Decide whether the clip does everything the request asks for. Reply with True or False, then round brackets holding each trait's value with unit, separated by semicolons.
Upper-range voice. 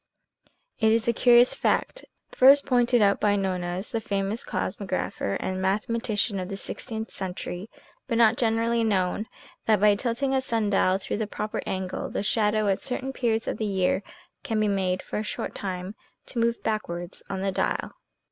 True (210 Hz)